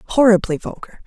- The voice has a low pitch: No, high, 210 Hz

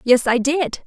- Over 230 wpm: No, fast, 210 wpm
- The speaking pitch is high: Yes, very high, 265 Hz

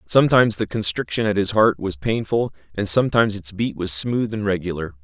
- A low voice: Yes, low, 100 Hz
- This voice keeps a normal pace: Yes, average, 190 wpm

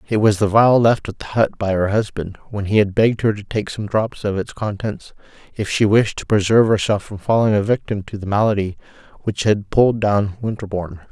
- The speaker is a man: Yes, male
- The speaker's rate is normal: No, fast, 220 wpm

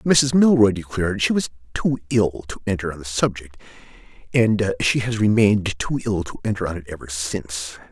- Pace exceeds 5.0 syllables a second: Yes, 5.4 syllables/s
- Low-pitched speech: Yes, low, 100 Hz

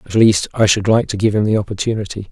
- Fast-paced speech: Yes, fast, 260 wpm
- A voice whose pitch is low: Yes, low, 105 Hz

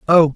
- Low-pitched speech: No, medium, 160 Hz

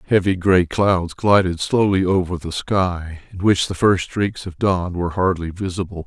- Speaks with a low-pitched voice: Yes, very low, 90 Hz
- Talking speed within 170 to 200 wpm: Yes, average, 180 wpm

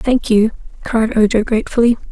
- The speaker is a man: No, female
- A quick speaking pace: No, average, 140 wpm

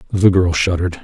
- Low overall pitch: Yes, very low, 90 Hz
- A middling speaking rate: Yes, average, 175 wpm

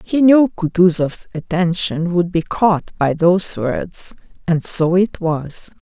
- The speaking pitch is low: No, medium, 180 Hz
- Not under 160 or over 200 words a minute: No, average, 145 wpm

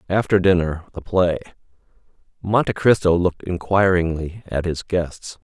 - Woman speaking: No, male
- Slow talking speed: Yes, slow, 120 wpm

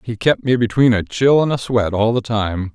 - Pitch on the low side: Yes, low, 115 Hz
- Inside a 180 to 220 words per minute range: No, fast, 260 wpm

